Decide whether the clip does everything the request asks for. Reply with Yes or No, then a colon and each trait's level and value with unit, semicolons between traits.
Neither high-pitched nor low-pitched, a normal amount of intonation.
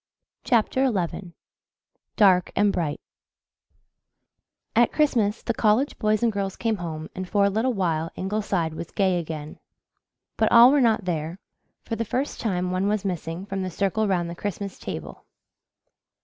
No: high, 195 Hz; average, 3.9 semitones